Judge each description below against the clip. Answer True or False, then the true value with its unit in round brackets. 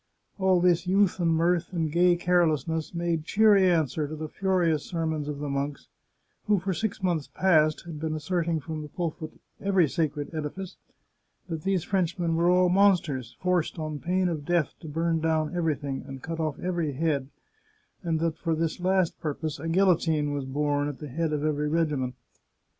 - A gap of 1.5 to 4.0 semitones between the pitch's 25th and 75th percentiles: True (2.8 semitones)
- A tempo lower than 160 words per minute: False (185 wpm)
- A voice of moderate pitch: True (165 Hz)